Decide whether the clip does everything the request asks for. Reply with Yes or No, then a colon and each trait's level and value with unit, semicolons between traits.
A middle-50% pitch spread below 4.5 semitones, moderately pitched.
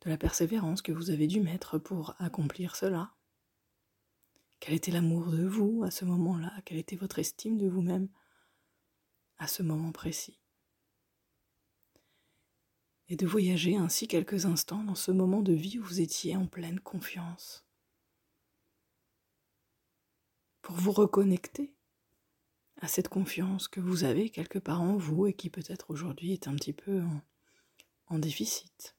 Yes: narrow, 2.6 semitones; medium, 180 Hz